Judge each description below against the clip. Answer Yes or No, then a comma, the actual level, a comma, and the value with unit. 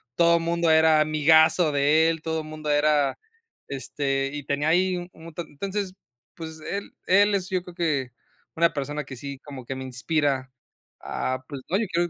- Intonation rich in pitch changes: No, average, 3.0 semitones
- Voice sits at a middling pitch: Yes, medium, 155 Hz